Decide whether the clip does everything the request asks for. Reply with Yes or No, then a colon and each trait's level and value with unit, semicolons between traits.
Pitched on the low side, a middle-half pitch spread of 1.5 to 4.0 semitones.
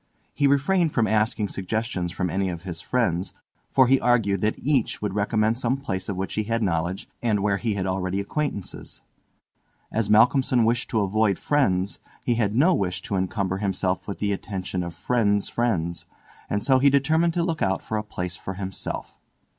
No: low, 105 Hz; average, 4.4 semitones